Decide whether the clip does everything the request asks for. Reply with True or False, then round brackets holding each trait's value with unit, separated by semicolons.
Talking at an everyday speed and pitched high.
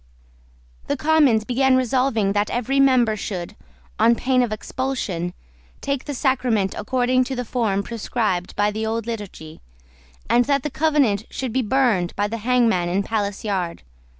True (160 wpm; 230 Hz)